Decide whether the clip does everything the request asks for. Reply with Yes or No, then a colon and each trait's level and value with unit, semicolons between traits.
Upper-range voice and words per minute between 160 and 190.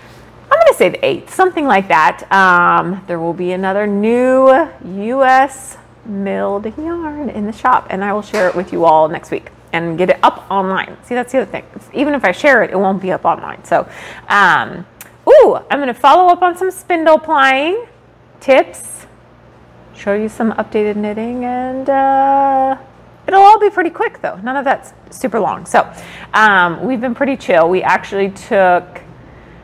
Yes: high, 230 Hz; average, 180 wpm